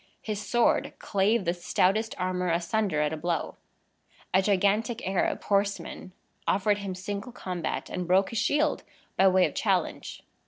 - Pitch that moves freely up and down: No, narrow, 2.5 semitones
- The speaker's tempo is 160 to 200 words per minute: No, average, 150 wpm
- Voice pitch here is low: No, high, 195 Hz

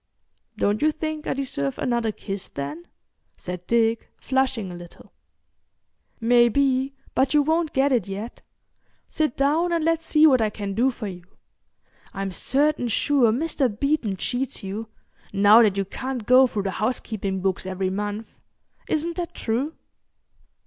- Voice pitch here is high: Yes, high, 235 Hz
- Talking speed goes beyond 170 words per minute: No, average, 150 wpm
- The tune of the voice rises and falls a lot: Yes, wide, 5.8 semitones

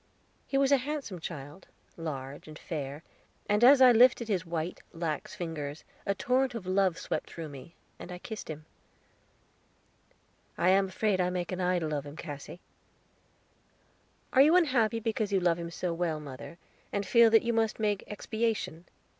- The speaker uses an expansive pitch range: Yes, wide, 5.7 semitones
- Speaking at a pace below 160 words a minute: No, average, 170 wpm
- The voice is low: No, medium, 185 Hz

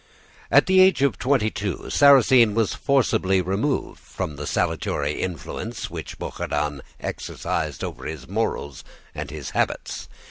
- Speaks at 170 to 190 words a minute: No, slow, 135 wpm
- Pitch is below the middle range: Yes, very low, 95 Hz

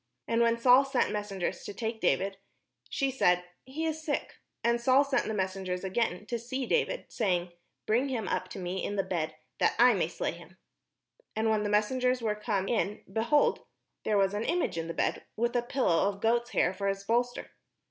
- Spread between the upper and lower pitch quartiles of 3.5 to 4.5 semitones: Yes, average, 4.1 semitones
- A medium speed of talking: No, fast, 210 wpm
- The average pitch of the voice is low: No, high, 220 Hz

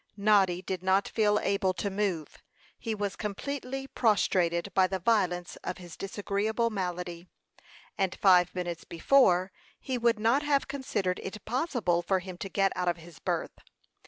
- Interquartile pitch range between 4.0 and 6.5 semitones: No, average, 3.5 semitones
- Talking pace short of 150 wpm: No, average, 160 wpm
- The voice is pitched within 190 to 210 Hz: Yes, high, 195 Hz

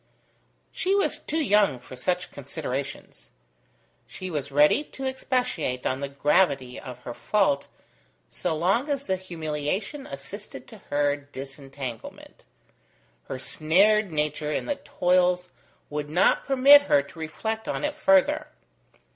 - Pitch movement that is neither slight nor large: No, wide, 6.9 semitones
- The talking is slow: Yes, slow, 130 wpm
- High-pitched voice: No, medium, 160 Hz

